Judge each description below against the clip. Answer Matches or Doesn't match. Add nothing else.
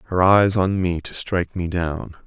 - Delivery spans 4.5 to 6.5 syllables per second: Matches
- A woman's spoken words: Doesn't match